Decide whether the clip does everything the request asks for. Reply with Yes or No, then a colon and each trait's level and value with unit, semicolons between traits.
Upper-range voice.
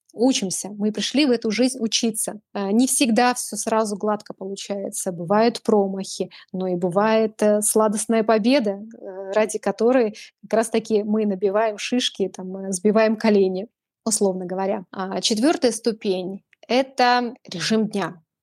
Yes: high, 215 Hz